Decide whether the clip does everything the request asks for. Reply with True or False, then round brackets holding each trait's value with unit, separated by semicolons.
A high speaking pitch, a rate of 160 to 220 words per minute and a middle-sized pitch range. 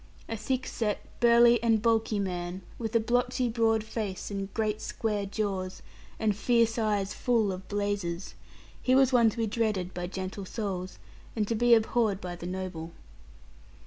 True (215 Hz; 165 wpm; 3.3 semitones)